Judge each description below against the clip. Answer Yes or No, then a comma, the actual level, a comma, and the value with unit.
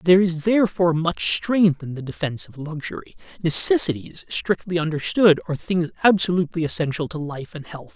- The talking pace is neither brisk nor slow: Yes, average, 160 wpm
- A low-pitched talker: No, medium, 165 Hz